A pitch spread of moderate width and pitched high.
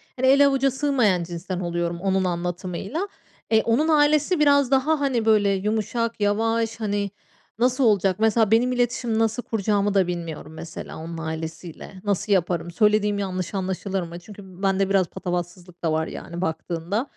Yes: average, 4.6 semitones; high, 200 Hz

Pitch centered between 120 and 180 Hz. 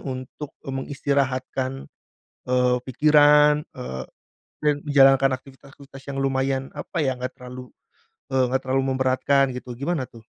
Yes: low, 135 Hz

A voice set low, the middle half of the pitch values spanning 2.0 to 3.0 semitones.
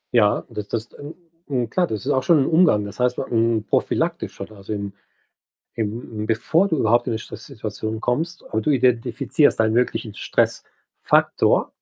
No: low, 115 Hz; average, 3.6 semitones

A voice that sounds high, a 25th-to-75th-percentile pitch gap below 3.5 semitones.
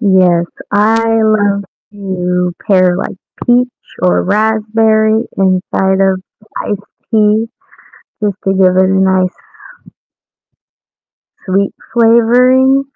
Yes: high, 200 Hz; average, 2.8 semitones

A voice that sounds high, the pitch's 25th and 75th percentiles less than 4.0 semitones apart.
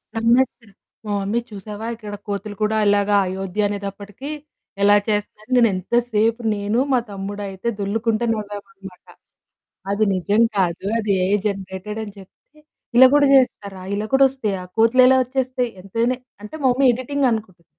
Yes: high, 210 Hz; average, 3.1 semitones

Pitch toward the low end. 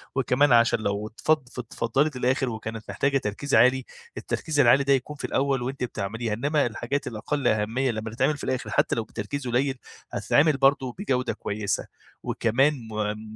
Yes: low, 125 Hz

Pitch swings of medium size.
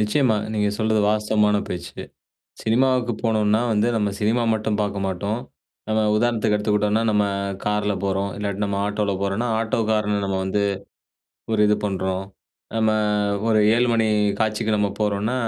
No: narrow, 1.2 semitones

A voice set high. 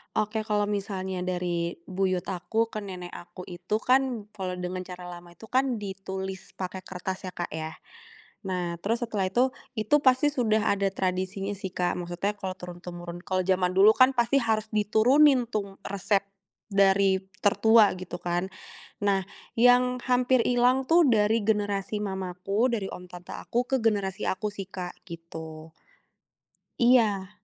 Yes: high, 195 Hz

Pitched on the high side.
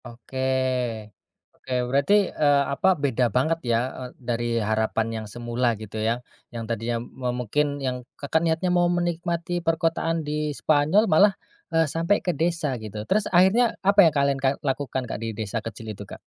No: medium, 140 Hz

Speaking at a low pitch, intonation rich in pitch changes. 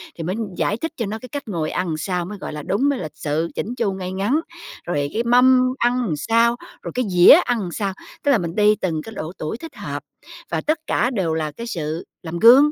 No: high, 200 Hz; wide, 6.3 semitones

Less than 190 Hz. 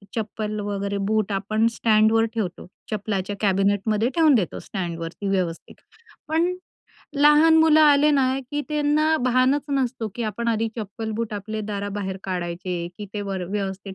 No: high, 215 Hz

